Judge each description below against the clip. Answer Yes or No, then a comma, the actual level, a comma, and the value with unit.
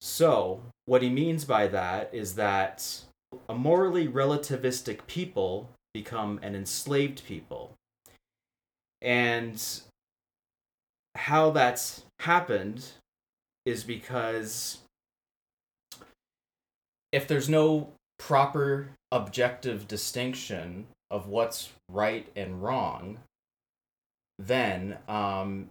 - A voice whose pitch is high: No, low, 120 Hz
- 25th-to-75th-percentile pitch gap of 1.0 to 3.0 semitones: No, average, 4.9 semitones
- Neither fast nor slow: No, slow, 80 wpm